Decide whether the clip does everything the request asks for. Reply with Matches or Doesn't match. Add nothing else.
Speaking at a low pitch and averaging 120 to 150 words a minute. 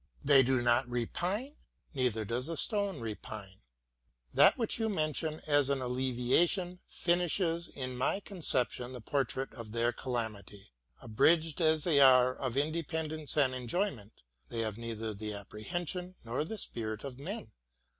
Matches